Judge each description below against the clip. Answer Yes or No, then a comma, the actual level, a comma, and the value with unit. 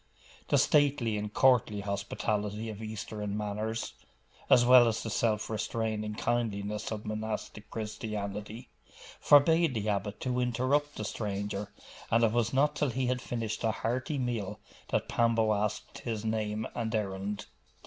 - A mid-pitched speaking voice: No, low, 110 Hz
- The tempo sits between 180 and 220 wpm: No, average, 145 wpm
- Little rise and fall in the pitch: Yes, narrow, 2.3 semitones